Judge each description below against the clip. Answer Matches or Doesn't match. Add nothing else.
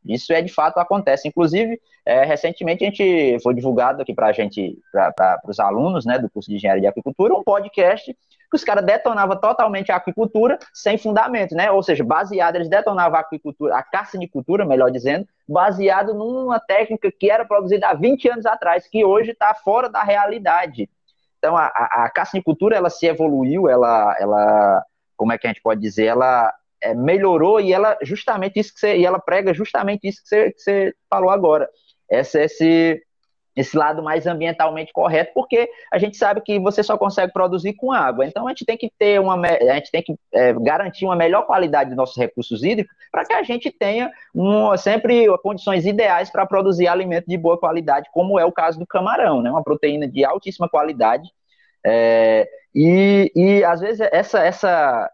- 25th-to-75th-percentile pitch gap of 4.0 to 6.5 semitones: Matches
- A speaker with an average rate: Doesn't match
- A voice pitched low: Doesn't match